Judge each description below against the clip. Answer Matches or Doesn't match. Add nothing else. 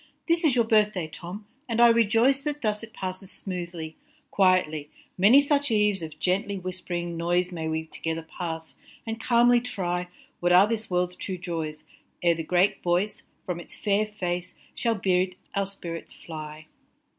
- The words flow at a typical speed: Matches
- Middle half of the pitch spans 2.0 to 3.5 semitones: Doesn't match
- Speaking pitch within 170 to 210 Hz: Matches